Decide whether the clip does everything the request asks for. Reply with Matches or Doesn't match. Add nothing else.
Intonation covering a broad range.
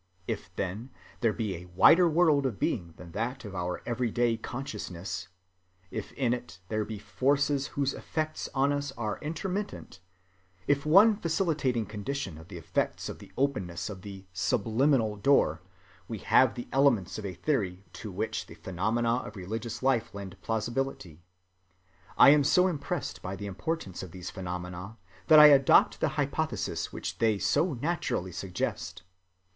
Matches